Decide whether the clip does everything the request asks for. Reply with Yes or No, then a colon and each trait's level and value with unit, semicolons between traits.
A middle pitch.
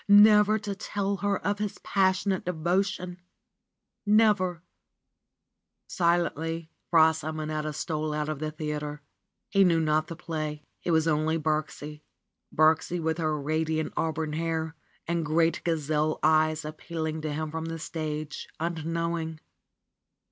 Yes: medium, 160 Hz